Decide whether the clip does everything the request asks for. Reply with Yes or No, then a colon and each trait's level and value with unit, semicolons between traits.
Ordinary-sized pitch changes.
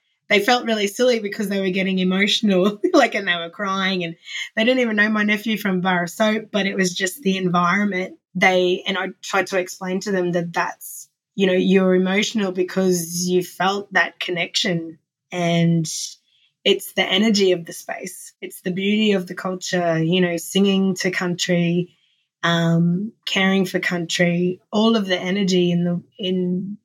No: narrow, 2.3 semitones